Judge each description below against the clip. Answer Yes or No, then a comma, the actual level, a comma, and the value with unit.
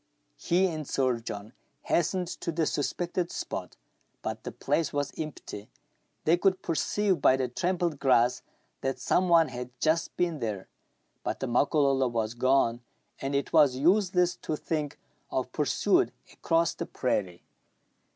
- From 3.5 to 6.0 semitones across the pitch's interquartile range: Yes, average, 5.1 semitones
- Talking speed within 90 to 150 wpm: Yes, average, 145 wpm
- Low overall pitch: No, medium, 150 Hz